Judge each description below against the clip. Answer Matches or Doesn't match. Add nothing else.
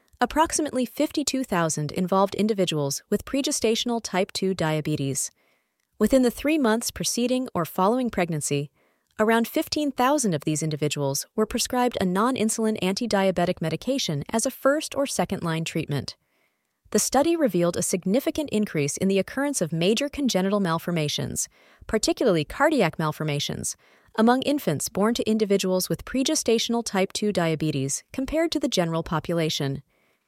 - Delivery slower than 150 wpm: Matches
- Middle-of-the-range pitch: Doesn't match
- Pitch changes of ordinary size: Doesn't match